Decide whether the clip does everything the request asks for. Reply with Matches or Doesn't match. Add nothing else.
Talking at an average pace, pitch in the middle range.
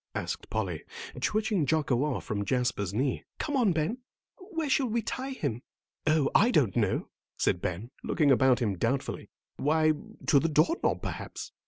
Matches